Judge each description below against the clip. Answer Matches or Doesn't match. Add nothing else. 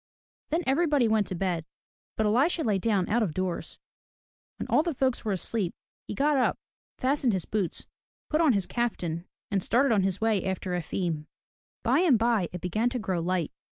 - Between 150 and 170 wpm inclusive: Doesn't match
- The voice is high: Matches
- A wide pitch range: Matches